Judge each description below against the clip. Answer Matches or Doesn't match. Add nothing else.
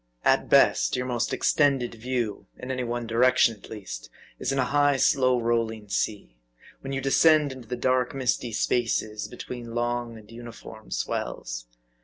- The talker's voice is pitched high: Doesn't match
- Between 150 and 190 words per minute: Matches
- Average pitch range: Doesn't match